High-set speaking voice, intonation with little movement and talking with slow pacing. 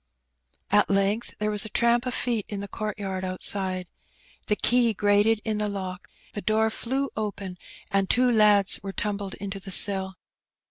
No: high, 205 Hz; narrow, 2.0 semitones; average, 175 wpm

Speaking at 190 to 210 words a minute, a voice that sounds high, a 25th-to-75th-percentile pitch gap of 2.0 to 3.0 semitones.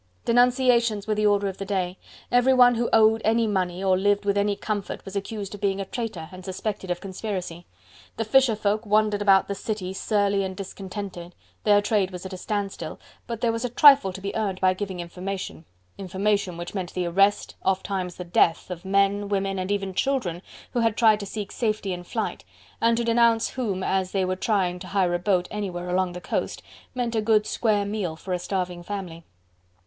Yes: fast, 205 wpm; high, 200 Hz; narrow, 2.6 semitones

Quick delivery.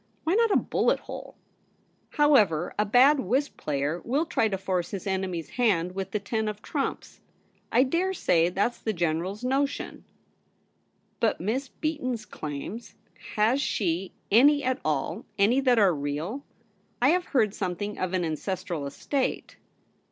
No: average, 155 wpm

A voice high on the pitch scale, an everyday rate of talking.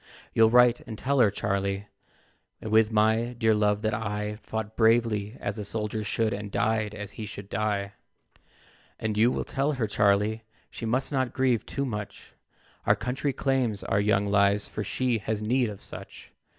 No: low, 110 Hz; average, 175 wpm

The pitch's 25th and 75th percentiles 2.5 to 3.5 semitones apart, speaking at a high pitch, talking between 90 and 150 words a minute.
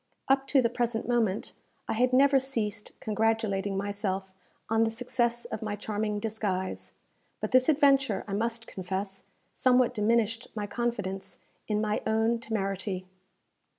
Yes: average, 2.8 semitones; high, 220 Hz; average, 140 wpm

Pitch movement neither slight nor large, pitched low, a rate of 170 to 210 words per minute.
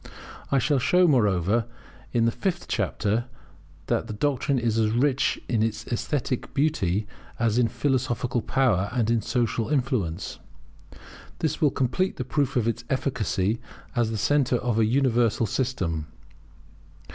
No: average, 3.7 semitones; low, 120 Hz; average, 140 wpm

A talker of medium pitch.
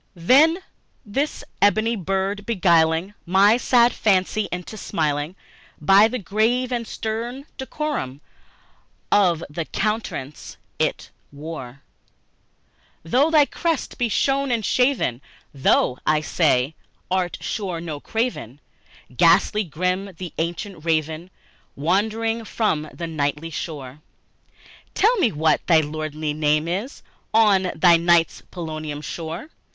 Yes: medium, 180 Hz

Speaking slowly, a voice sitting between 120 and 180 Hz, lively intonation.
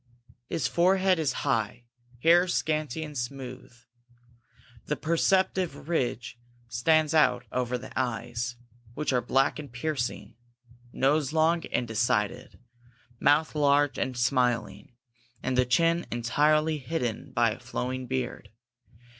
No: slow, 120 wpm; low, 135 Hz; average, 4.3 semitones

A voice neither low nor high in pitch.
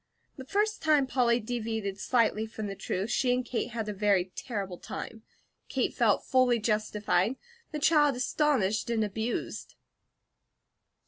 No: high, 230 Hz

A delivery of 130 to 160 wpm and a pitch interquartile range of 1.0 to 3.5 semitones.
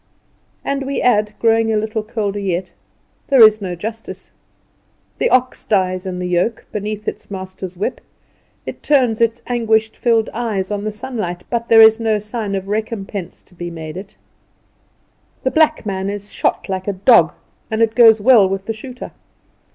No: average, 175 wpm; average, 3.0 semitones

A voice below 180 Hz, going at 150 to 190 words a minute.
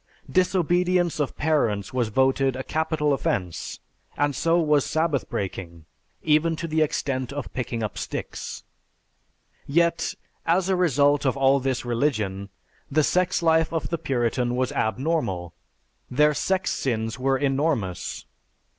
No: medium, 140 Hz; slow, 135 wpm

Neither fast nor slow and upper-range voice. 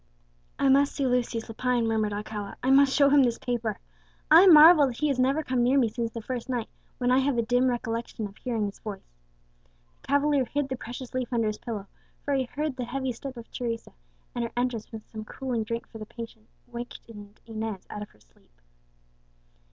No: fast, 210 wpm; high, 240 Hz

